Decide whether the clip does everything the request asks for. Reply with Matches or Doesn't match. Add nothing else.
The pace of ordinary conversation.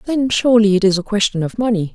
Doesn't match